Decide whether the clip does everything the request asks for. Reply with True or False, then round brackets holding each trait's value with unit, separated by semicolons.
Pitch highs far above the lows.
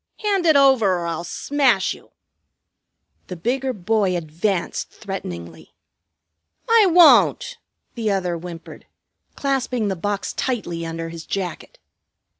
True (7.7 semitones)